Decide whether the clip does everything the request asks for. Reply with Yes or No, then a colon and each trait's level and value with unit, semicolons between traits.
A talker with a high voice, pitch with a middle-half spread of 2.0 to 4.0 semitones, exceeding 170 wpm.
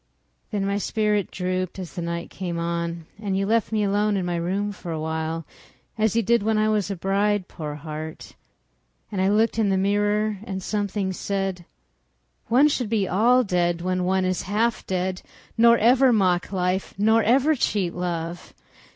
Yes: high, 195 Hz; average, 3.1 semitones; average, 180 wpm